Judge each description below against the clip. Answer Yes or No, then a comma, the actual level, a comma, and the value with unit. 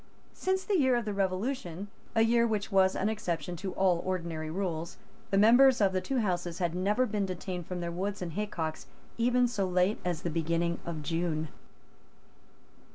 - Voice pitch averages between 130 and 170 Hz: No, medium, 185 Hz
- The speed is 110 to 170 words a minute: No, average, 180 wpm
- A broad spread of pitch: No, average, 4.0 semitones